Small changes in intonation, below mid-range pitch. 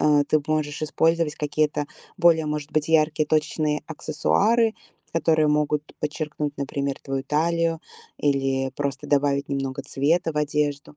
No: narrow, 1.6 semitones; medium, 150 Hz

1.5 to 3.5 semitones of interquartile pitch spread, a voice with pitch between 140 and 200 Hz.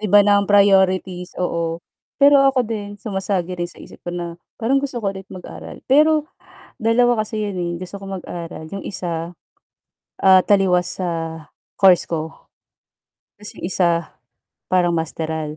Yes: average, 3.1 semitones; high, 190 Hz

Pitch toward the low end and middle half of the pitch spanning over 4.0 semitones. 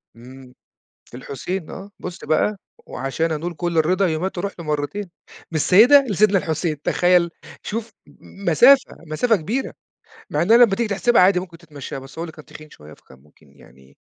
No: medium, 170 Hz; average, 5.0 semitones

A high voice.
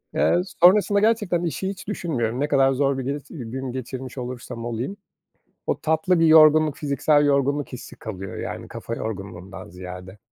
No: low, 135 Hz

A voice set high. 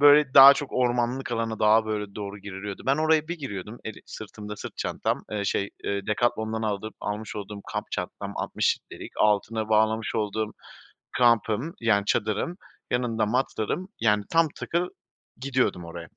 No: low, 110 Hz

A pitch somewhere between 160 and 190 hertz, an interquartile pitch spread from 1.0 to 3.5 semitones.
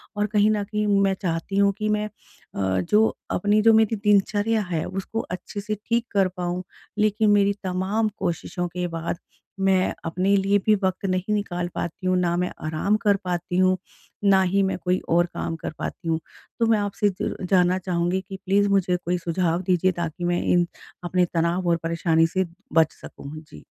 Yes: medium, 185 Hz; narrow, 2.6 semitones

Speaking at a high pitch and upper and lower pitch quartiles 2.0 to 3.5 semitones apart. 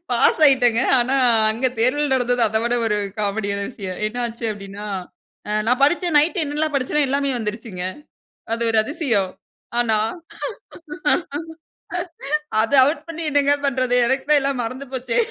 No: high, 245 Hz; average, 4.1 semitones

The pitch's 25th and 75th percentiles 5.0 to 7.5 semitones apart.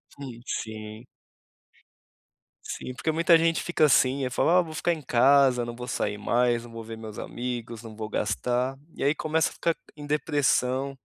No: average, 4.1 semitones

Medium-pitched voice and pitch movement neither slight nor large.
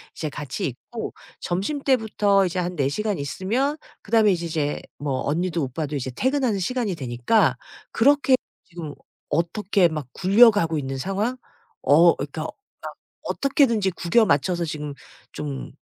No: medium, 175 Hz; wide, 6.6 semitones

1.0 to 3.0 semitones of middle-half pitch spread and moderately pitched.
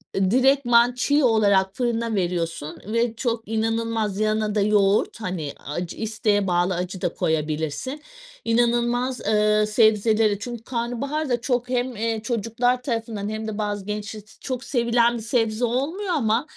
No: average, 2.7 semitones; high, 225 Hz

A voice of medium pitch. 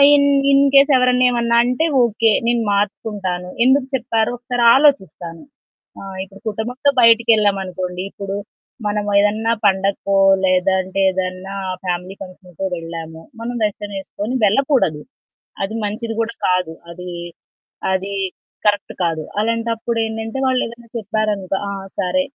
No: high, 210 Hz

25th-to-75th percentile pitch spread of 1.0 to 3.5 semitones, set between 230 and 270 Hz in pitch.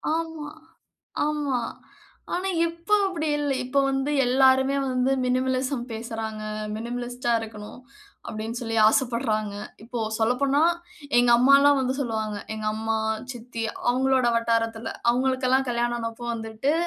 Yes: average, 2.9 semitones; high, 245 Hz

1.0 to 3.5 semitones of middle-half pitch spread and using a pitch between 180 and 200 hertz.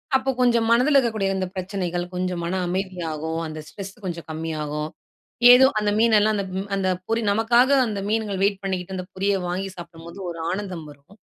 No: average, 3.9 semitones; high, 190 Hz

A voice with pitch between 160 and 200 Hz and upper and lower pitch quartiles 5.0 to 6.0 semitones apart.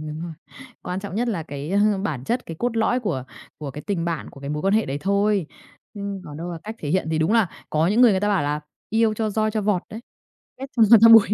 Yes: high, 195 Hz; wide, 5.4 semitones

